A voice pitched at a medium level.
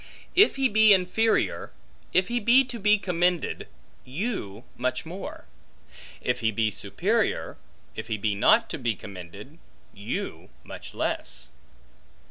Yes: medium, 165 Hz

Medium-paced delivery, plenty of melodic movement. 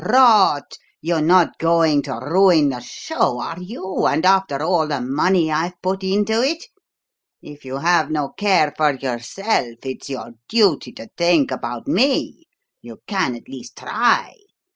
Yes: average, 155 wpm; wide, 5.8 semitones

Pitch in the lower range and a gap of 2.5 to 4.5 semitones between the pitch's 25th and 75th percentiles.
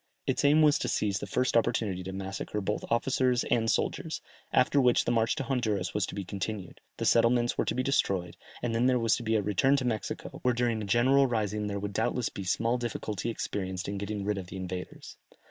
Yes: low, 110 Hz; average, 3.7 semitones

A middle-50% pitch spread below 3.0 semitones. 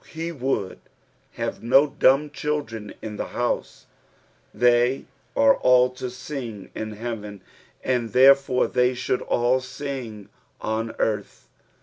No: average, 3.3 semitones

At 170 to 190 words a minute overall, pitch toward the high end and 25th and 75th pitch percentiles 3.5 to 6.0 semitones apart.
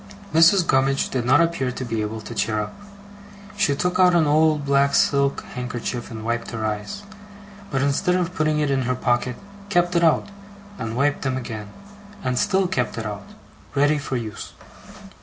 No: average, 180 wpm; low, 135 Hz; average, 5.2 semitones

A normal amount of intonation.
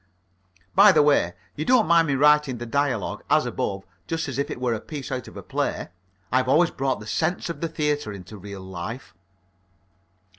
No: wide, 5.8 semitones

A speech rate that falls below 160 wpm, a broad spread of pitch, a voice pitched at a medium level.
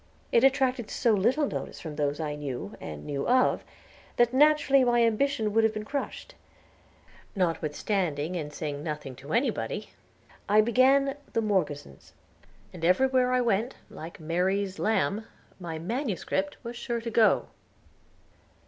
No: average, 140 wpm; wide, 7.8 semitones; high, 215 Hz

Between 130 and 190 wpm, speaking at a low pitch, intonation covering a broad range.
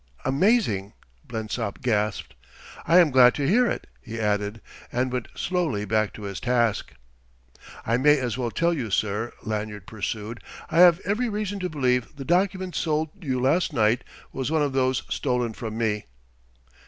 Yes: average, 165 wpm; low, 125 Hz; wide, 6.5 semitones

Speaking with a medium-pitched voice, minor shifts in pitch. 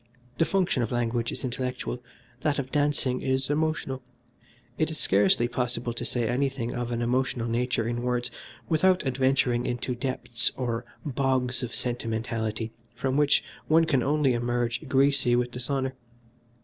No: low, 125 Hz; narrow, 2.1 semitones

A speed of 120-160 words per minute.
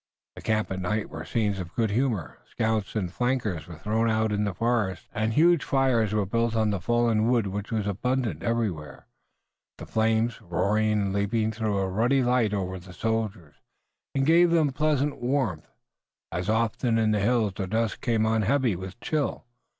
No: average, 180 wpm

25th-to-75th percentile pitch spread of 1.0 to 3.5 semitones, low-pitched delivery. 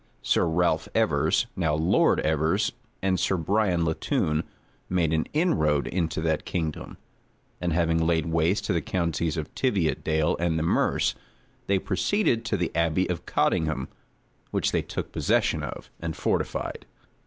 Yes: narrow, 2.6 semitones; very low, 85 Hz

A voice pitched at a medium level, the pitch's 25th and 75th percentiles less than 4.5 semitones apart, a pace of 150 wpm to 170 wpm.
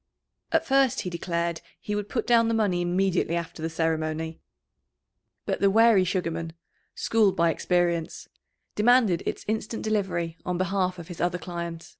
Yes: medium, 180 Hz; average, 3.6 semitones; average, 155 wpm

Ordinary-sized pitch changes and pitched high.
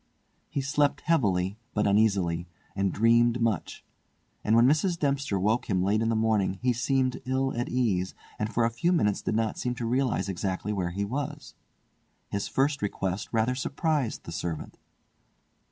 No: average, 4.8 semitones; low, 115 Hz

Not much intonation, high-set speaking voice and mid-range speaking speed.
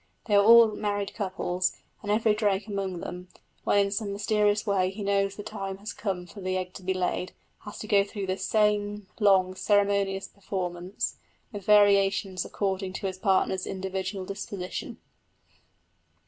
Yes: narrow, 1.7 semitones; high, 200 Hz; average, 160 wpm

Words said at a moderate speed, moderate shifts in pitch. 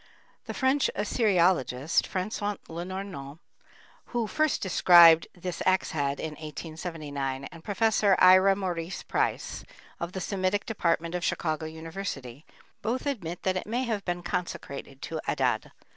No: slow, 130 wpm; average, 3.8 semitones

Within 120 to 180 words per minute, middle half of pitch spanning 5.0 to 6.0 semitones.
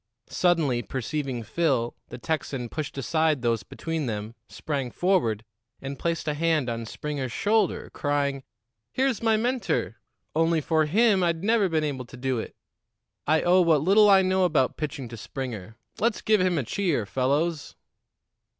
Yes: average, 160 wpm; wide, 5.5 semitones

